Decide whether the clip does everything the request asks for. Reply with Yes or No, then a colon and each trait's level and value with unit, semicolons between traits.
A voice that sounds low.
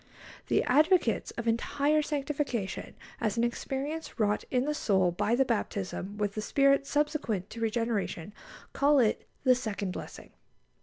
No: high, 235 Hz